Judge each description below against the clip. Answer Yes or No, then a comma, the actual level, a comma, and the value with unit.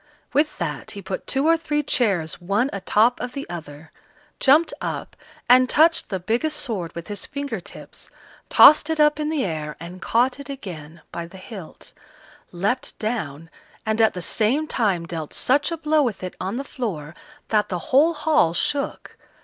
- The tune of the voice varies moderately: No, wide, 8.4 semitones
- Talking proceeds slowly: No, average, 180 wpm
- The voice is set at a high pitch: Yes, high, 220 Hz